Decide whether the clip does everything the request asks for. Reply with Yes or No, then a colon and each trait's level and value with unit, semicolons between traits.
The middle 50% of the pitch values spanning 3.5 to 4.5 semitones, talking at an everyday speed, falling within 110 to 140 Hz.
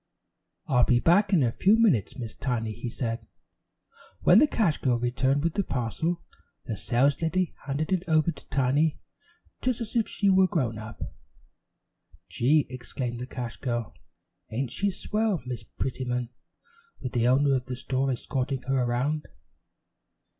No: average, 5.2 semitones; average, 155 wpm; low, 135 Hz